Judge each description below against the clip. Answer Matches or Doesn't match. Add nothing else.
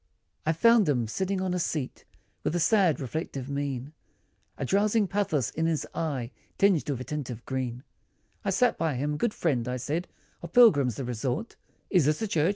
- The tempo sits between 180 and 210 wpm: Matches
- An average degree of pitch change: Doesn't match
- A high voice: Doesn't match